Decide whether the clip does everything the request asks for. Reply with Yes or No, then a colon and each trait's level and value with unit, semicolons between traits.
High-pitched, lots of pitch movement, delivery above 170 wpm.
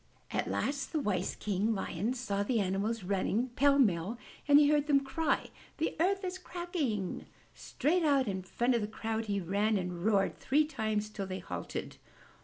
Yes: high, 225 Hz; wide, 6.3 semitones; average, 185 wpm